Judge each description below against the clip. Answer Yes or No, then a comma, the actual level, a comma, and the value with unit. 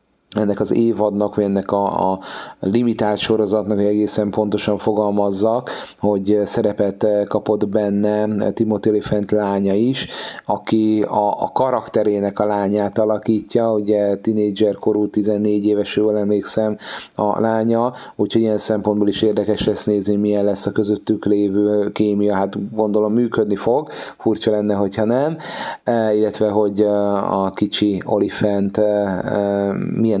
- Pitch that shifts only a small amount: Yes, narrow, 1.0 semitones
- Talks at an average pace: Yes, average, 135 wpm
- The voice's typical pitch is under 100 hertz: No, low, 105 Hz